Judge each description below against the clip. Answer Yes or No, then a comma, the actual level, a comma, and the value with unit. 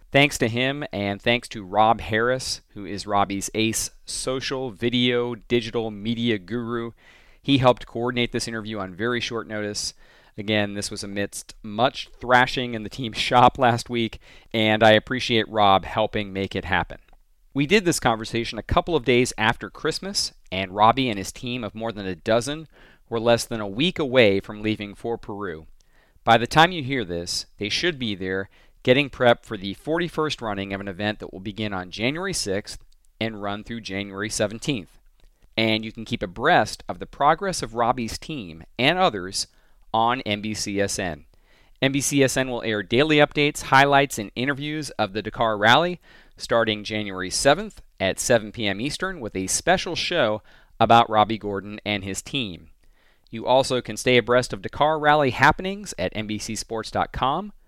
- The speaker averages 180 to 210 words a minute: No, average, 165 wpm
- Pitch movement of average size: Yes, average, 3.7 semitones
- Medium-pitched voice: No, low, 115 Hz